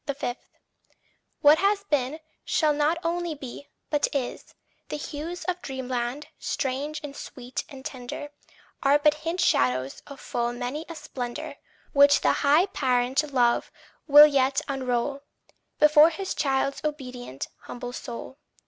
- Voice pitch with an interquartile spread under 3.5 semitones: Yes, average, 3.1 semitones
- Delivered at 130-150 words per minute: Yes, slow, 135 wpm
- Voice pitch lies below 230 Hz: No, very high, 280 Hz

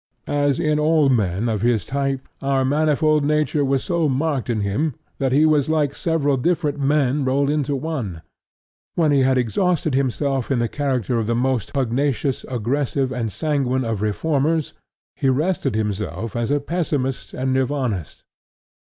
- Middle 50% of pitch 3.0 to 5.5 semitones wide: Yes, average, 3.3 semitones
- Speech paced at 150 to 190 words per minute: Yes, average, 160 wpm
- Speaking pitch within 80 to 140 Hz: Yes, low, 135 Hz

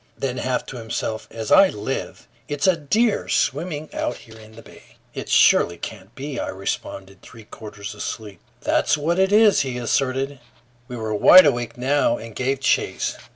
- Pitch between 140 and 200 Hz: No, low, 125 Hz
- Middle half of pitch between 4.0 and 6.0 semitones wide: Yes, average, 4.8 semitones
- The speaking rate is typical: Yes, average, 175 wpm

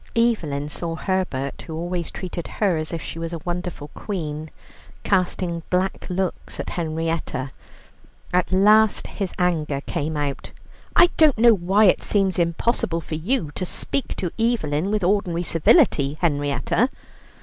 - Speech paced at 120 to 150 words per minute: Yes, average, 145 wpm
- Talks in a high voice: No, medium, 175 Hz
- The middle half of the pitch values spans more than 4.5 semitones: No, average, 3.8 semitones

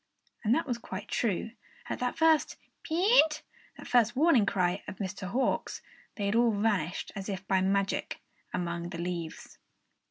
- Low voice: No, high, 205 Hz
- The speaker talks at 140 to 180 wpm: Yes, average, 155 wpm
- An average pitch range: Yes, average, 4.8 semitones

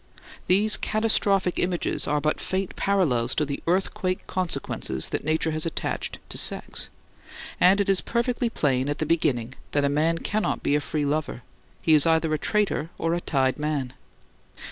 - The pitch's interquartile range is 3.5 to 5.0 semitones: Yes, average, 4.5 semitones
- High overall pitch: No, medium, 160 Hz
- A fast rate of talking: No, average, 170 wpm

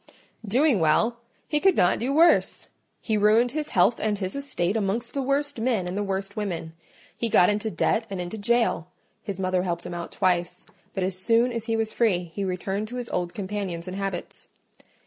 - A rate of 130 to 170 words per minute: No, average, 200 wpm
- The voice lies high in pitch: Yes, high, 205 Hz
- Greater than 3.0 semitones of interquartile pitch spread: Yes, average, 4.3 semitones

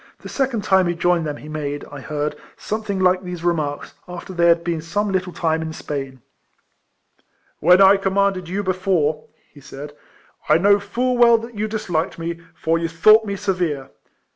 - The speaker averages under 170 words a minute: No, average, 190 wpm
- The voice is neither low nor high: Yes, medium, 175 Hz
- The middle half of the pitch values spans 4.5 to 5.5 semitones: No, average, 4.0 semitones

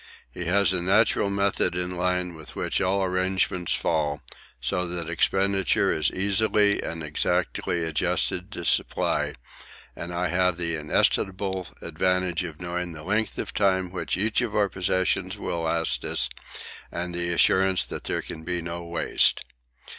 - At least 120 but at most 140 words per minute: No, average, 155 wpm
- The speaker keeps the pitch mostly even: Yes, narrow, 2.1 semitones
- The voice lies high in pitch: No, very low, 90 Hz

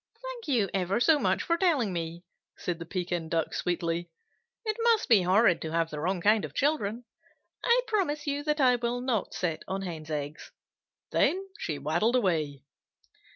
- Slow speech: No, average, 175 wpm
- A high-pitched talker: Yes, high, 195 Hz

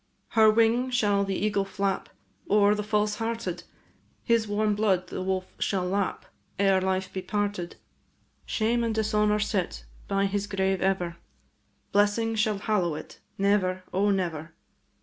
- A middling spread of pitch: No, narrow, 2.1 semitones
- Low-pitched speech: No, high, 200 Hz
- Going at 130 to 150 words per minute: Yes, average, 145 wpm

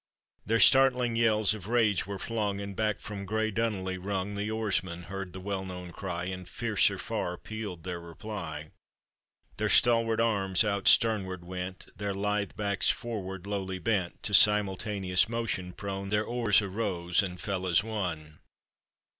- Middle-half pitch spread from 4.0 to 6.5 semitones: No, average, 2.7 semitones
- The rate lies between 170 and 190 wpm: No, average, 155 wpm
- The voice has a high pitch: No, low, 100 Hz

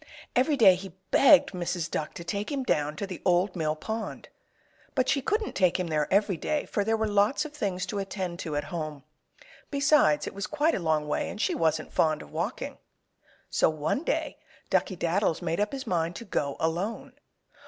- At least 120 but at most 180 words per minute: No, average, 200 wpm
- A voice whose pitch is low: No, medium, 185 Hz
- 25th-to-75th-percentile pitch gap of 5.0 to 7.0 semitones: Yes, wide, 5.6 semitones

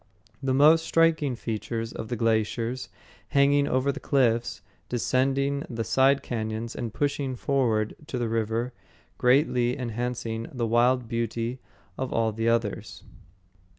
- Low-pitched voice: Yes, low, 120 Hz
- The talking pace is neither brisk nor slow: No, slow, 130 wpm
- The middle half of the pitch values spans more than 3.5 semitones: No, average, 2.8 semitones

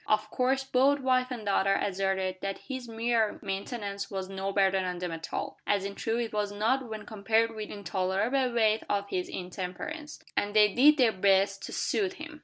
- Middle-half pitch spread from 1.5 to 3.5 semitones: No, average, 4.0 semitones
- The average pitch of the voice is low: No, high, 210 Hz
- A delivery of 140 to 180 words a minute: No, average, 200 wpm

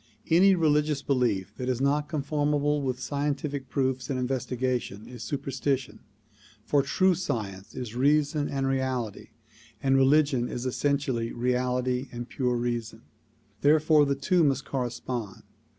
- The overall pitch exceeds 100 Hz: Yes, low, 135 Hz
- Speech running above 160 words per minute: No, slow, 135 wpm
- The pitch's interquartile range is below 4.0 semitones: Yes, average, 2.7 semitones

